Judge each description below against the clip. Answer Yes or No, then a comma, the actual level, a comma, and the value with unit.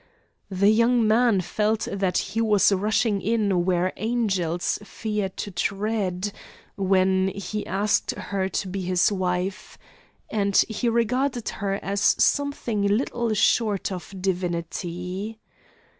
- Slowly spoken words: Yes, slow, 120 wpm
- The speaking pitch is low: No, high, 200 Hz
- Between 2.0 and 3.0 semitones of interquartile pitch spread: Yes, average, 2.7 semitones